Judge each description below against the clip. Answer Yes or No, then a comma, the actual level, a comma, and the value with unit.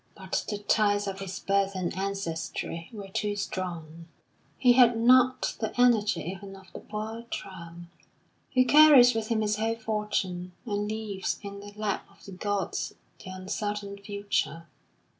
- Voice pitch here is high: Yes, high, 205 Hz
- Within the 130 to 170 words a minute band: Yes, average, 155 wpm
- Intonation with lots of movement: No, narrow, 2.5 semitones